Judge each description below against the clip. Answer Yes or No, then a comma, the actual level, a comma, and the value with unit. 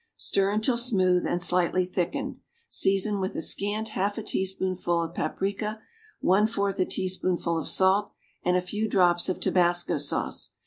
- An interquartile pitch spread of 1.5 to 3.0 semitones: Yes, narrow, 2.5 semitones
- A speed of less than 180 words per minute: Yes, average, 160 wpm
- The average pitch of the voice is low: No, high, 190 Hz